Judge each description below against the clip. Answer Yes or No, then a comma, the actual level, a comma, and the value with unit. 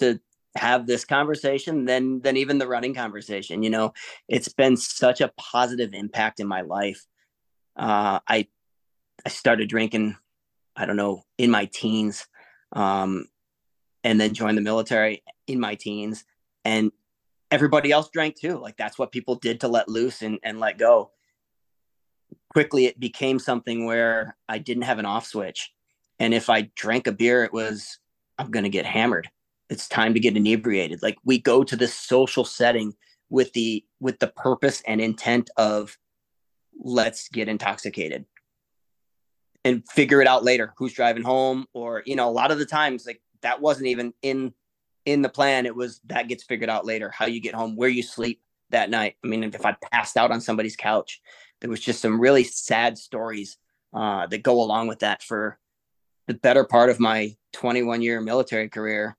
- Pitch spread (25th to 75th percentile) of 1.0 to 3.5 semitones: Yes, average, 2.8 semitones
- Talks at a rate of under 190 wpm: Yes, average, 180 wpm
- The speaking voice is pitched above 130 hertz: No, low, 115 Hz